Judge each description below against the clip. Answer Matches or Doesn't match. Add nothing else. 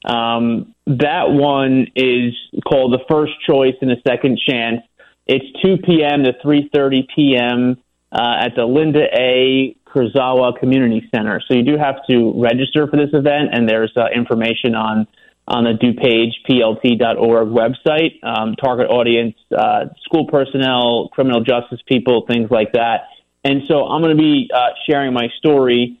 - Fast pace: Doesn't match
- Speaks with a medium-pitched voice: Doesn't match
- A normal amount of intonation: Matches